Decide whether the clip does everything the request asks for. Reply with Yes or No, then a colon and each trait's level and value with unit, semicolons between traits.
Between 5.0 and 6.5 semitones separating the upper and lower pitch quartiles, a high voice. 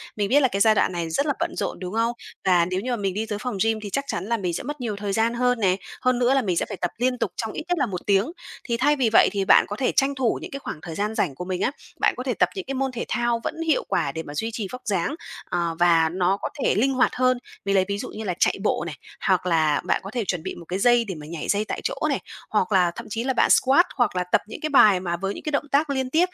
Yes: wide, 5.5 semitones; high, 215 Hz